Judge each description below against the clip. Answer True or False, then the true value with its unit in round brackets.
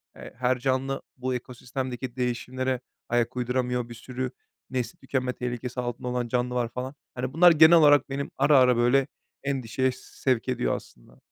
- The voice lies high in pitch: False (125 Hz)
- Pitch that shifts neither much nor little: False (1.3 semitones)